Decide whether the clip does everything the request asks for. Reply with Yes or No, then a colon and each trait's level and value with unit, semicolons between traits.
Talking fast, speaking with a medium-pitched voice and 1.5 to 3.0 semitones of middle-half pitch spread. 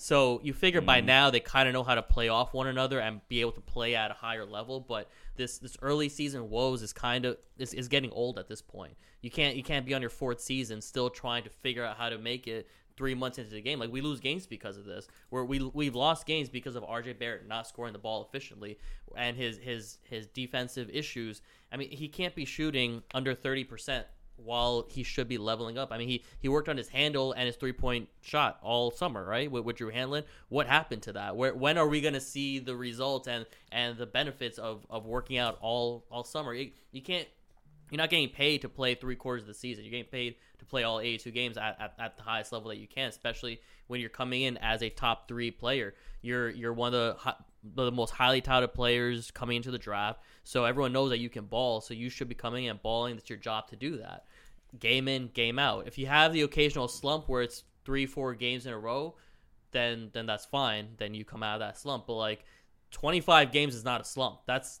No: fast, 240 wpm; low, 125 Hz; narrow, 2.6 semitones